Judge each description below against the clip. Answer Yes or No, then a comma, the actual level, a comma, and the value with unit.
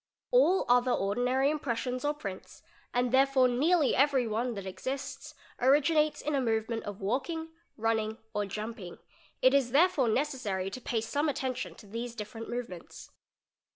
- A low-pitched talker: No, very high, 250 Hz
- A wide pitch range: No, average, 4.0 semitones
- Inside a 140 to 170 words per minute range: Yes, average, 155 wpm